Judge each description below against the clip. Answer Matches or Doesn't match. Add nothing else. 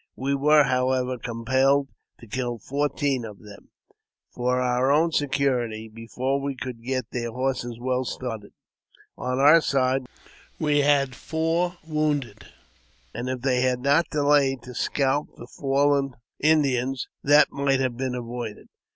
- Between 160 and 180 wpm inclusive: Doesn't match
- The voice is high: Doesn't match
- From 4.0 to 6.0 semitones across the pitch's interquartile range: Doesn't match